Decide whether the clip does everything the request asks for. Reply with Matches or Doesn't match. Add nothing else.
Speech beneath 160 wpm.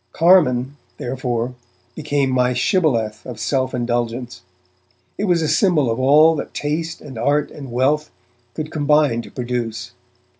Matches